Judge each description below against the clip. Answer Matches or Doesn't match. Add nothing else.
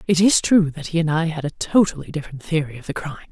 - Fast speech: Matches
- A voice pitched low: Doesn't match